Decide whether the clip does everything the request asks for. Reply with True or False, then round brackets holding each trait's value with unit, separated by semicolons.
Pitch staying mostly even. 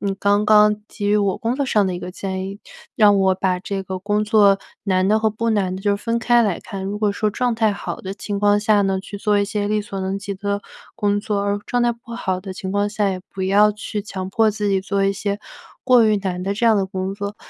True (1.5 semitones)